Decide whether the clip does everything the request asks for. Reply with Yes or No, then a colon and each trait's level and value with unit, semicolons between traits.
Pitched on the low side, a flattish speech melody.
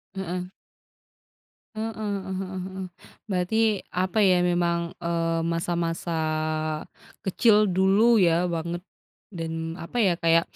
No: medium, 180 Hz; narrow, 2.2 semitones